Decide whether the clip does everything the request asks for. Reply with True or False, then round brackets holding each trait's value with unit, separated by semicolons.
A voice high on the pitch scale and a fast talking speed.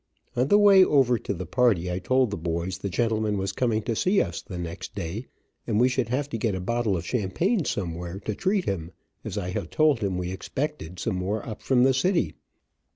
False (110 Hz; 225 wpm)